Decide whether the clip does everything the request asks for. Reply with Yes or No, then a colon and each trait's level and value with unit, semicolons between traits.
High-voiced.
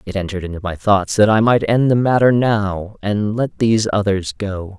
No: low, 105 Hz